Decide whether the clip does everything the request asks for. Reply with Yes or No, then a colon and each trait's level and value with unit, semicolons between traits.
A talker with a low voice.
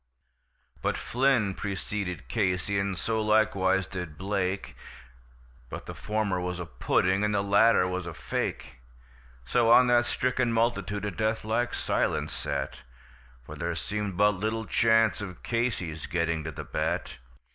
Yes: low, 100 Hz